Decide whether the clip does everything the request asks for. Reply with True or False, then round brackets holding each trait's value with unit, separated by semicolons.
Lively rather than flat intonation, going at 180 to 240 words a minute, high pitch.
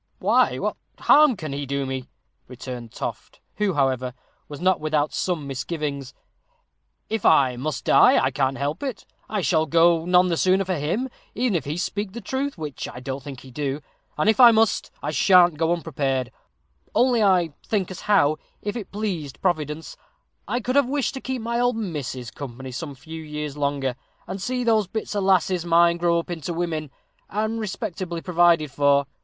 False (6.1 semitones; 185 wpm; 170 Hz)